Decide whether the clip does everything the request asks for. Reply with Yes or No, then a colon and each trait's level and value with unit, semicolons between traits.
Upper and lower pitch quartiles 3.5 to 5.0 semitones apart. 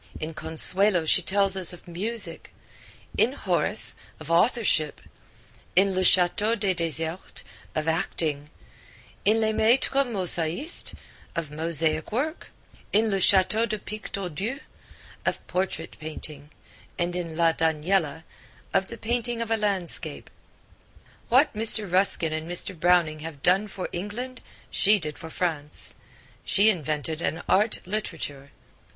Yes: average, 4.7 semitones